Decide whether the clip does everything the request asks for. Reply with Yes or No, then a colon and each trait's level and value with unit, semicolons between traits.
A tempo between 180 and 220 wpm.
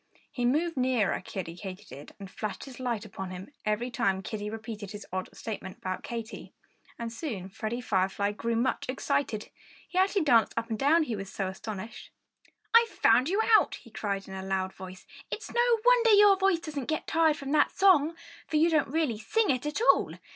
Yes: average, 195 wpm